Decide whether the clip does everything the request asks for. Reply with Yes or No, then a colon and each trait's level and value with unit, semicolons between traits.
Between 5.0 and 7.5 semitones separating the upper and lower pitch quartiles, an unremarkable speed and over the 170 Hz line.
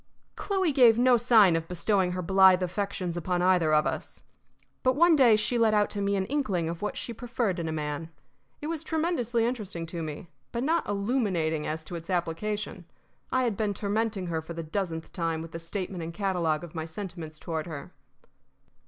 Yes: wide, 5.4 semitones; average, 195 wpm; high, 190 Hz